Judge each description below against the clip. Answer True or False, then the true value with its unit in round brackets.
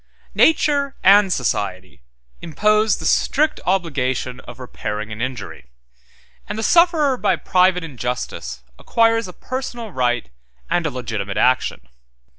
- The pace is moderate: False (120 wpm)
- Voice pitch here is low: False (165 Hz)